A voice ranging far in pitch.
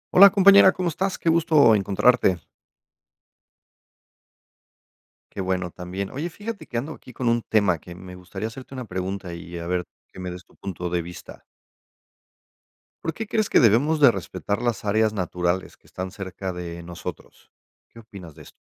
Yes: wide, 6.6 semitones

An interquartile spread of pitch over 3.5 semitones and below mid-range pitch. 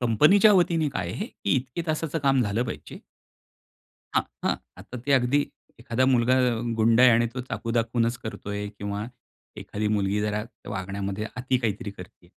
Yes: average, 4.2 semitones; low, 115 Hz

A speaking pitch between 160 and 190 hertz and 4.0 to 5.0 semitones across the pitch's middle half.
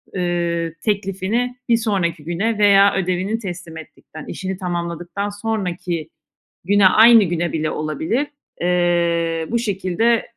No: medium, 185 Hz; average, 3.3 semitones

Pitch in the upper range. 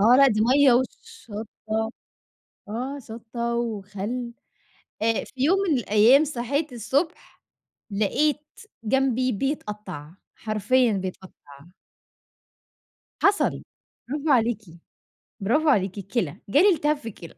Yes: high, 235 Hz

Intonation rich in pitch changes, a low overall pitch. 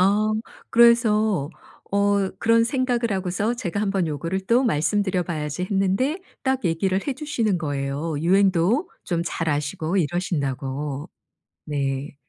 No: wide, 5.9 semitones; high, 190 Hz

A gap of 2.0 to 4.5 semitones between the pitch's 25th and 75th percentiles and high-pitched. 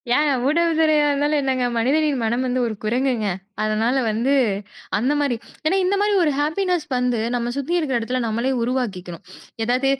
Yes: average, 4.2 semitones; very high, 260 Hz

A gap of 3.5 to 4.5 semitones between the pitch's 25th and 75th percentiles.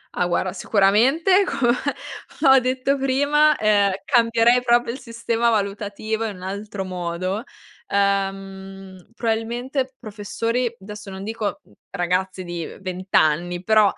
Yes: average, 3.8 semitones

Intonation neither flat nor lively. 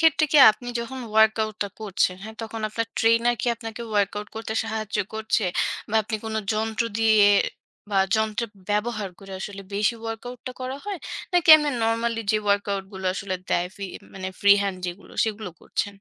No: narrow, 2.1 semitones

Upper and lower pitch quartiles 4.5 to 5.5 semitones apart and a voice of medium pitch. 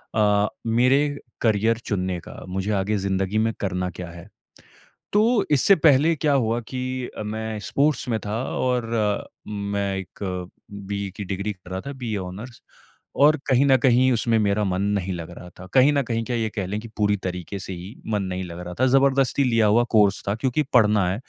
No: average, 4.8 semitones; low, 110 Hz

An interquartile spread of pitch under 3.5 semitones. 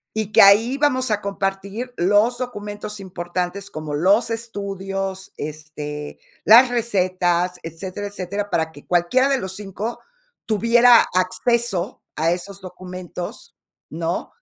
No: average, 3.9 semitones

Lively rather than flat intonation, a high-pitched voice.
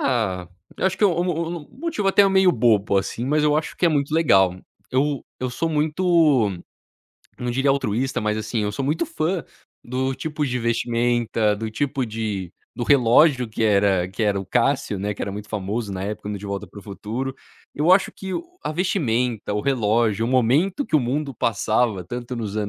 No: wide, 5.9 semitones; low, 120 Hz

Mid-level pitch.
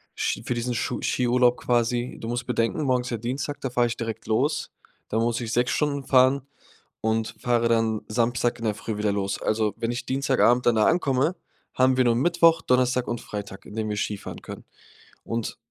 No: low, 120 Hz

